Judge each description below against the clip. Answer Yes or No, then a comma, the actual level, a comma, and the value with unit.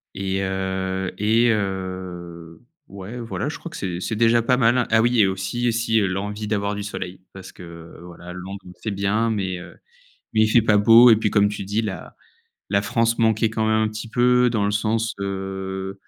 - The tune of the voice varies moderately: Yes, average, 3.0 semitones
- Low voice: Yes, low, 105 Hz